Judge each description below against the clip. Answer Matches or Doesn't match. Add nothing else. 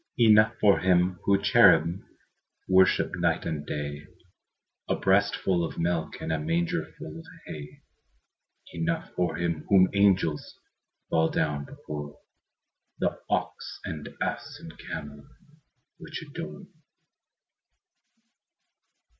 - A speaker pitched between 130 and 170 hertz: Doesn't match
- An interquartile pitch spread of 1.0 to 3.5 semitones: Doesn't match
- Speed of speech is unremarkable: Doesn't match